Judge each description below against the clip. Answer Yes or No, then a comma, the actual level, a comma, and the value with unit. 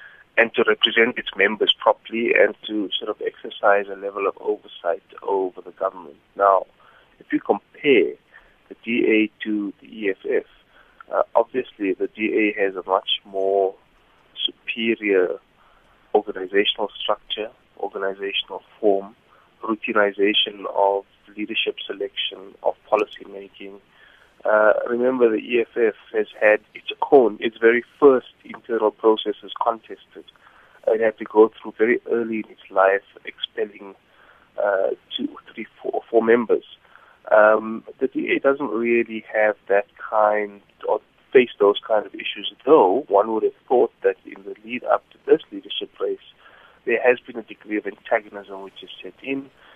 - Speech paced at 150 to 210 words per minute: No, average, 140 wpm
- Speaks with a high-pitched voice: No, low, 135 Hz